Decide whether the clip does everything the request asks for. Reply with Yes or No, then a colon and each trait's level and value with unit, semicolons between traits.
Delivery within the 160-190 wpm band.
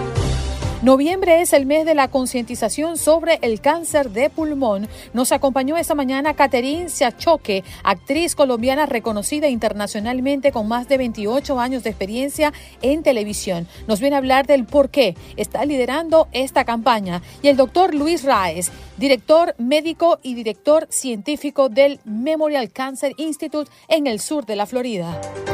No: average, 145 wpm